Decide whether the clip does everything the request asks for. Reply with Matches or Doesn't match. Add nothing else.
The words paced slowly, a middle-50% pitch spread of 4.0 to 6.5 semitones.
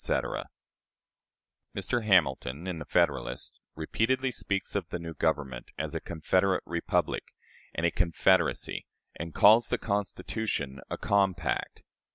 Matches